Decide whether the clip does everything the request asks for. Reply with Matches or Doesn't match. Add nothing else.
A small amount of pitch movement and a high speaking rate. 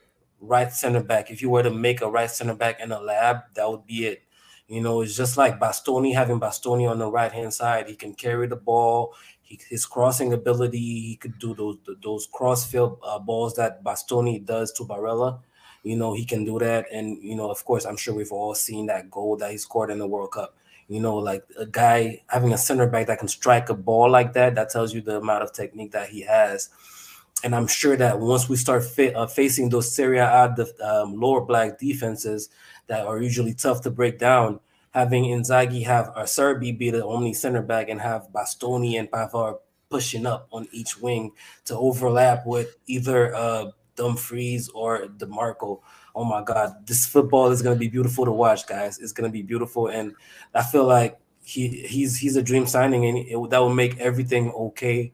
Matches